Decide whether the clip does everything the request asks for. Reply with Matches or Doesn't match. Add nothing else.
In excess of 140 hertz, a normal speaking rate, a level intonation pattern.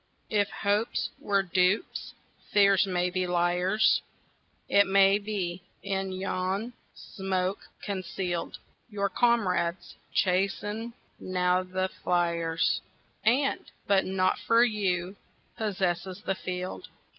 Doesn't match